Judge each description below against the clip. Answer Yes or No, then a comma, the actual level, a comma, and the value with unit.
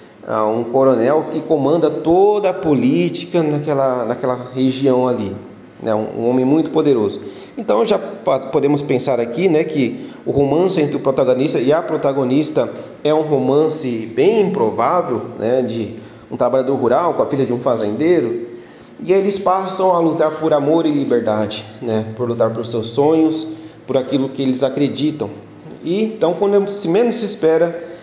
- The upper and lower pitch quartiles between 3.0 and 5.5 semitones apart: Yes, average, 4.4 semitones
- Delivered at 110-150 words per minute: No, average, 160 wpm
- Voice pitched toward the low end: No, medium, 145 Hz